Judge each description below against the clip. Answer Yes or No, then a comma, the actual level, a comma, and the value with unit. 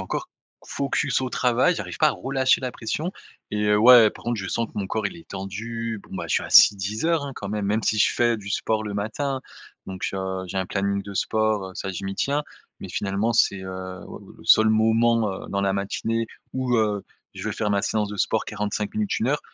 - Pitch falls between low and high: No, low, 110 Hz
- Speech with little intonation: No, average, 3.2 semitones